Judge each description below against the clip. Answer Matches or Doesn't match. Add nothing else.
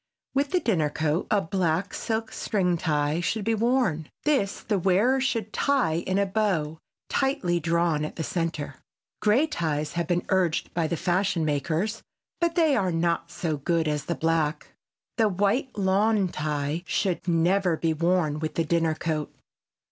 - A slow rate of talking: Doesn't match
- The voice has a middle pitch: Matches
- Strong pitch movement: Doesn't match